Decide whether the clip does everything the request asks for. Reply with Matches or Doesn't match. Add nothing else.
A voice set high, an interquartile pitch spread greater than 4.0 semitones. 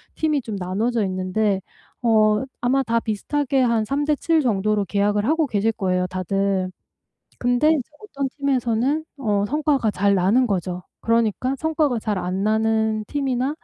Matches